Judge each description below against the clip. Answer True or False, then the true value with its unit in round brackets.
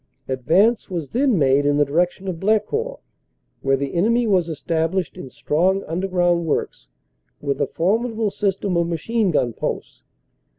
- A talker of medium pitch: True (180 Hz)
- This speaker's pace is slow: False (155 wpm)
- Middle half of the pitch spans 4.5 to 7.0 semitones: True (4.8 semitones)